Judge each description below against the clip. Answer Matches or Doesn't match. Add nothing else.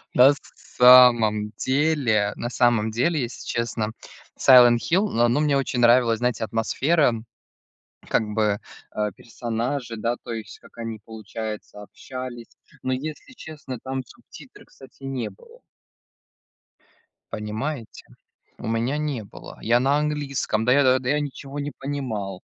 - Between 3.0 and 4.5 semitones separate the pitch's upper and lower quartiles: Matches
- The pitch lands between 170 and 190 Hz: Doesn't match